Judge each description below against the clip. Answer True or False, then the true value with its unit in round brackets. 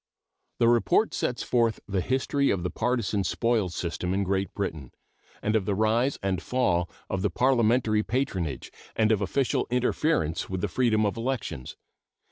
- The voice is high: False (110 Hz)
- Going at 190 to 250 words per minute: False (160 wpm)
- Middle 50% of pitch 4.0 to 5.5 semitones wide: True (4.6 semitones)